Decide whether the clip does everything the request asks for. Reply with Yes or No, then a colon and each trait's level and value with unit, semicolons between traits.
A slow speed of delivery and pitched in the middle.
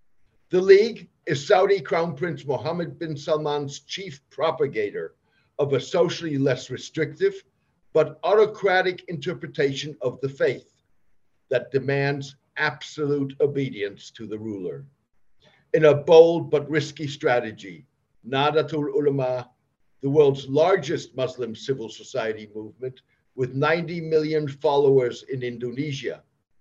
Yes: slow, 115 wpm; medium, 145 Hz